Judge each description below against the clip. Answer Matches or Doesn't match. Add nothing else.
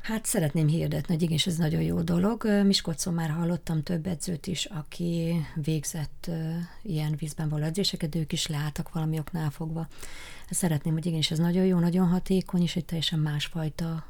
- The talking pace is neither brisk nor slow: Doesn't match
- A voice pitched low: Doesn't match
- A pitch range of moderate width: Doesn't match